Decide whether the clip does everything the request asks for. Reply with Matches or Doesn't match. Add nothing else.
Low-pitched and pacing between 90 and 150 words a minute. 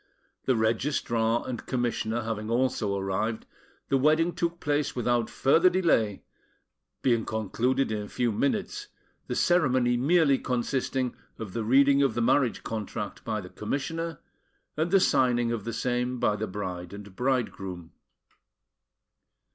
Matches